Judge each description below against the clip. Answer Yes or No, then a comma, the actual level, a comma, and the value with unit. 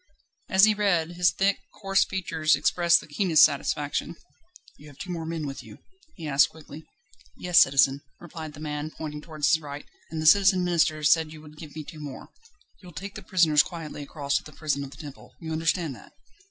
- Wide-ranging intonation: No, average, 2.8 semitones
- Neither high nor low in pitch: Yes, medium, 155 Hz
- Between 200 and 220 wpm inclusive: Yes, fast, 205 wpm